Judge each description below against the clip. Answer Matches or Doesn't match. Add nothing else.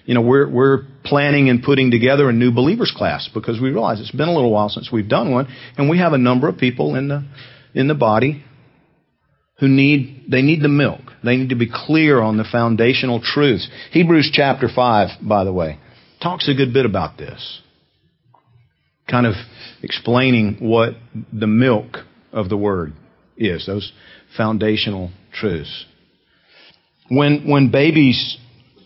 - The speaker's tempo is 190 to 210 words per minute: Doesn't match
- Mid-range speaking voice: Doesn't match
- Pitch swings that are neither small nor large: Matches